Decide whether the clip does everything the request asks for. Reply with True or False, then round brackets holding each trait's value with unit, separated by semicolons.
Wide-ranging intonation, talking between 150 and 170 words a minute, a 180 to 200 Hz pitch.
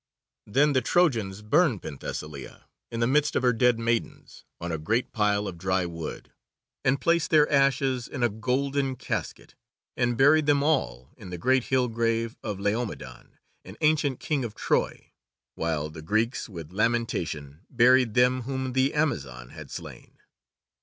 False (5.9 semitones; 160 wpm; 115 Hz)